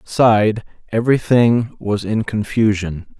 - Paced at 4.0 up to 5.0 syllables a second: Yes, 4.3 syllables/s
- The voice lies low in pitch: Yes, low, 110 Hz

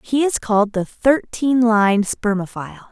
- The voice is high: Yes, high, 225 Hz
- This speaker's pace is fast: No, average, 145 wpm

